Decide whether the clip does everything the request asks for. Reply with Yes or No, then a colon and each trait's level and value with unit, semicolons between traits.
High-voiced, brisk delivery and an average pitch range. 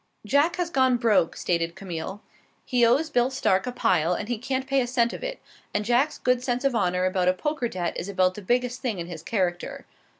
No: high, 235 Hz; fast, 220 wpm; wide, 5.9 semitones